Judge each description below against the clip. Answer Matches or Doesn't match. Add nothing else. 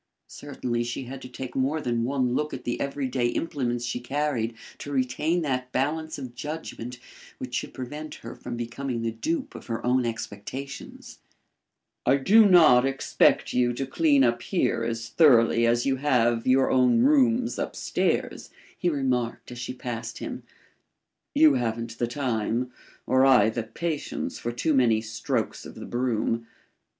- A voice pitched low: Matches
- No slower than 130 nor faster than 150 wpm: Doesn't match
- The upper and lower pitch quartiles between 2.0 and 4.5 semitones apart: Matches